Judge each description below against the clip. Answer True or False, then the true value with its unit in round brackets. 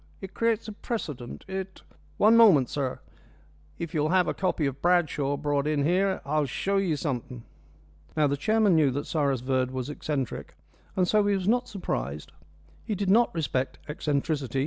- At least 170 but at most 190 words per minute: True (175 wpm)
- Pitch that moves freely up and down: True (5.8 semitones)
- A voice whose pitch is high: False (155 Hz)